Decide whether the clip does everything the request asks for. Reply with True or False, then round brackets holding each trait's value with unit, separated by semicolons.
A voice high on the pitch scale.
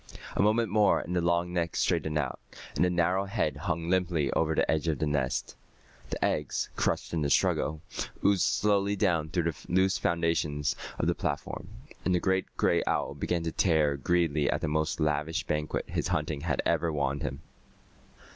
False (85 Hz)